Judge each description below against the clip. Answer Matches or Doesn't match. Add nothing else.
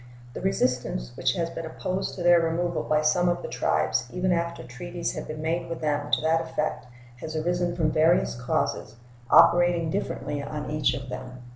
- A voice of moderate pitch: Matches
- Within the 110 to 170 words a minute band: Doesn't match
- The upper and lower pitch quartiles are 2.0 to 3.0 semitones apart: Doesn't match